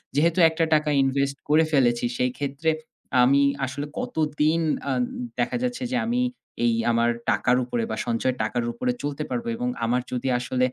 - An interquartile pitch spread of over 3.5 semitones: Yes, average, 4.5 semitones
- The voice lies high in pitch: No, medium, 140 Hz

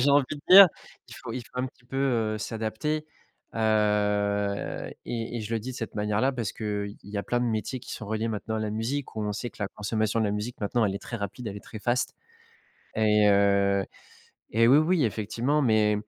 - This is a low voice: Yes, low, 110 Hz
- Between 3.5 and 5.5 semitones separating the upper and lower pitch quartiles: No, average, 3.0 semitones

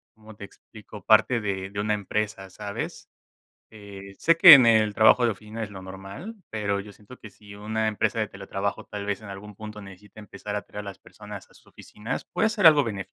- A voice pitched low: Yes, low, 105 Hz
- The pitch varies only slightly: Yes, narrow, 1.7 semitones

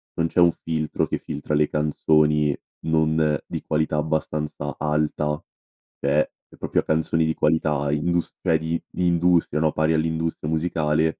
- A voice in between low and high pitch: No, very low, 80 Hz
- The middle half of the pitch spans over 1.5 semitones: No, narrow, 1.1 semitones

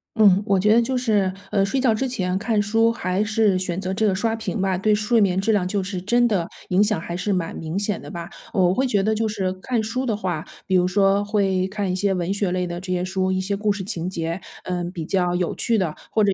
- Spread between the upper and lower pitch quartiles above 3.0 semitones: No, average, 2.7 semitones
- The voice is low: No, high, 195 Hz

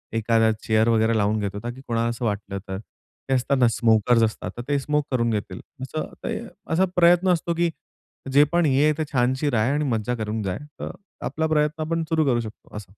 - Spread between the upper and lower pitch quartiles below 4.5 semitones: No, wide, 5.4 semitones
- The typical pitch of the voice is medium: No, low, 120 Hz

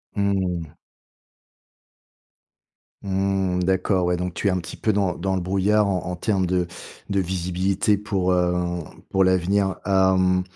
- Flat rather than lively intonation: Yes, narrow, 1.4 semitones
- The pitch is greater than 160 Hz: No, very low, 95 Hz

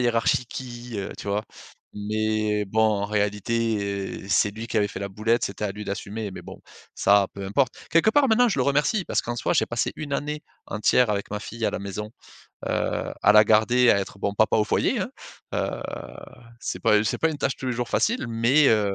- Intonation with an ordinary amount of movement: Yes, average, 3.3 semitones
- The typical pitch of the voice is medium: No, low, 110 Hz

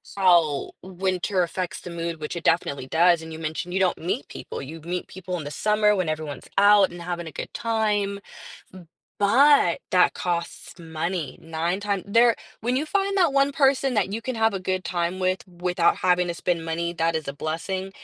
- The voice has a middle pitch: Yes, medium, 180 Hz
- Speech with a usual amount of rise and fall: Yes, average, 3.4 semitones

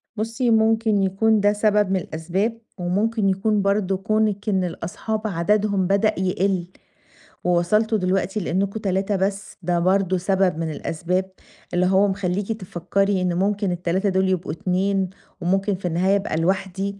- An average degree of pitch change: No, narrow, 2.2 semitones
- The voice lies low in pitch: No, high, 195 Hz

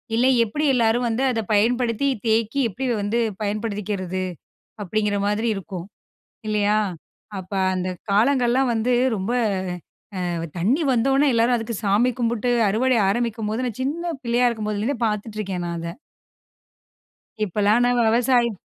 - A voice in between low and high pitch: No, high, 225 Hz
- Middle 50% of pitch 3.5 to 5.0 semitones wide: No, average, 3.0 semitones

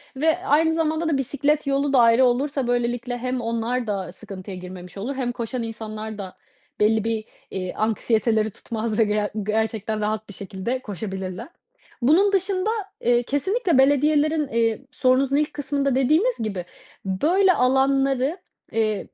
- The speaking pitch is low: No, high, 245 Hz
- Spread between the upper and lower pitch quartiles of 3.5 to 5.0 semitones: Yes, average, 4.7 semitones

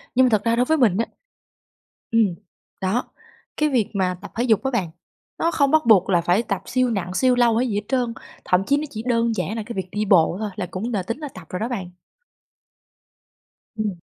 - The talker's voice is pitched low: No, high, 220 Hz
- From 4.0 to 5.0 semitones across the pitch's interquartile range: Yes, average, 4.5 semitones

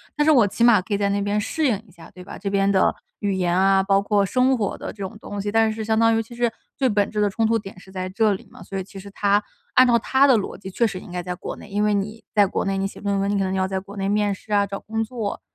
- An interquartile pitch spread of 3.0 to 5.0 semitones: No, narrow, 2.4 semitones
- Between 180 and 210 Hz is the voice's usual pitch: Yes, high, 205 Hz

